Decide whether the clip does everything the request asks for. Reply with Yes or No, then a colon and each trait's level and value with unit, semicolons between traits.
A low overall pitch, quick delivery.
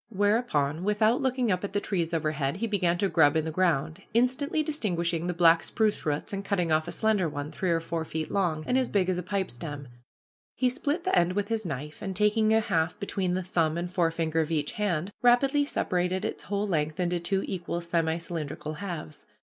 No: medium, 180 Hz; fast, 210 wpm